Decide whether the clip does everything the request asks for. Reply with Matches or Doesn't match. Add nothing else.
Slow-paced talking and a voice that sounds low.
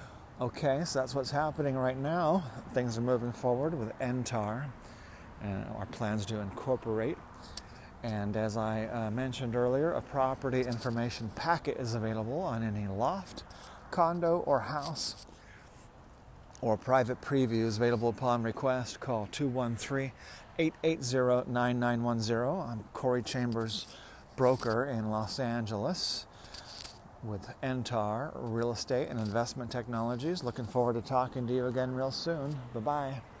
Matches